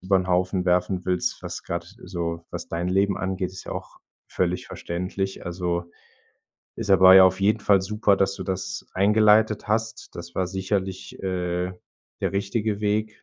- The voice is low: Yes, very low, 95 Hz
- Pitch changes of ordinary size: No, narrow, 2.0 semitones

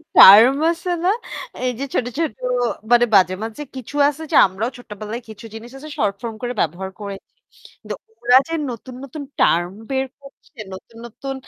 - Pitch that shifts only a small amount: No, average, 4.6 semitones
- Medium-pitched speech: No, high, 240 Hz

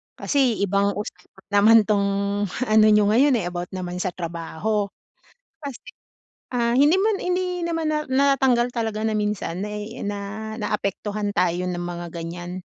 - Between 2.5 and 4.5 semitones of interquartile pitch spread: No, wide, 5.4 semitones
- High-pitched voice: Yes, high, 210 Hz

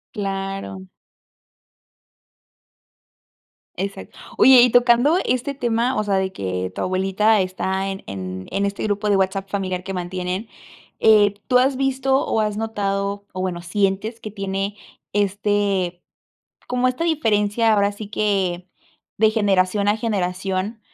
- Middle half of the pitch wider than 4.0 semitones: No, average, 2.7 semitones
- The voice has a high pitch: Yes, high, 200 Hz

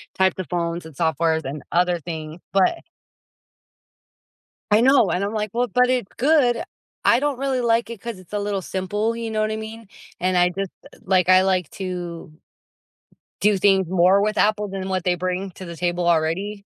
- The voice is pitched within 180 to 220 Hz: Yes, high, 190 Hz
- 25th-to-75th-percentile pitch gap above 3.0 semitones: Yes, average, 3.6 semitones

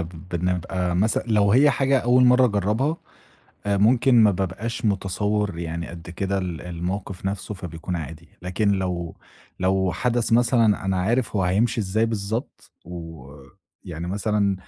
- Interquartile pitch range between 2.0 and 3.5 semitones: No, average, 3.9 semitones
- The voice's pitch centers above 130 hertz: No, very low, 95 Hz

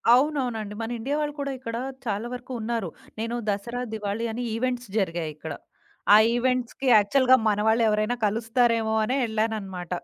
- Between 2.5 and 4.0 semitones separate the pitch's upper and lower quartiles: Yes, average, 2.8 semitones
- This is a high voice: Yes, high, 225 Hz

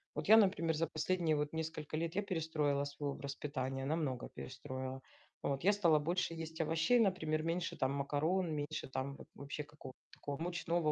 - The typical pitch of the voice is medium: Yes, medium, 155 Hz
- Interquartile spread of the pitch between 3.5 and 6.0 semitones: No, average, 3.0 semitones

